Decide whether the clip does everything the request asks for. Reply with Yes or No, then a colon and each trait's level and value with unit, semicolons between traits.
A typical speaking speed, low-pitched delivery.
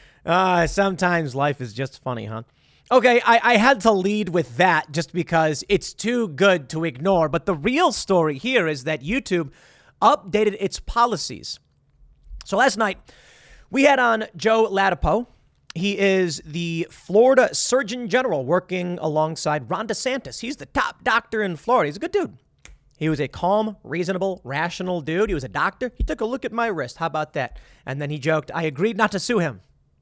No: average, 185 wpm; medium, 185 Hz